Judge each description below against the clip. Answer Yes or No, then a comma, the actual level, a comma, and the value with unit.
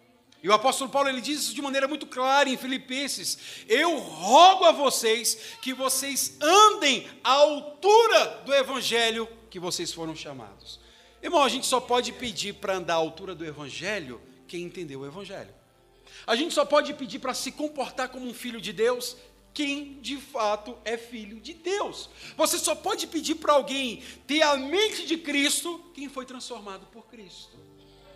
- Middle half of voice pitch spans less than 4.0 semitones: No, average, 5.2 semitones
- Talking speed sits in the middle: Yes, average, 170 wpm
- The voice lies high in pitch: Yes, very high, 260 Hz